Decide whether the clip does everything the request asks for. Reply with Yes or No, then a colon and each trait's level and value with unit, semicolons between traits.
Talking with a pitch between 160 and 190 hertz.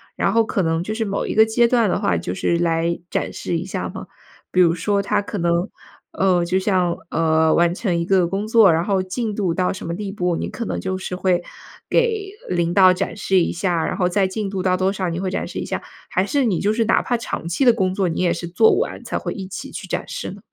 Yes: medium, 185 Hz